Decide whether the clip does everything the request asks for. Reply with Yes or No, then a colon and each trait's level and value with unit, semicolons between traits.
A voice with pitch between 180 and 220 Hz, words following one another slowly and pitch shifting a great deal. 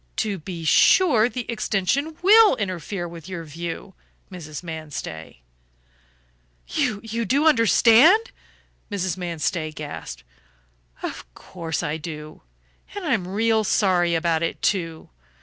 Yes: medium, 185 Hz; slow, 115 wpm; wide, 5.8 semitones